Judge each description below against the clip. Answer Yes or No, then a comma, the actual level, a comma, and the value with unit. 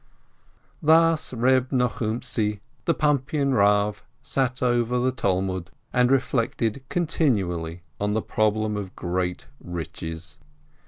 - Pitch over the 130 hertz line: No, low, 115 Hz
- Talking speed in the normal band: No, slow, 105 wpm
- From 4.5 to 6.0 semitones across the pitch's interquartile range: Yes, average, 5.2 semitones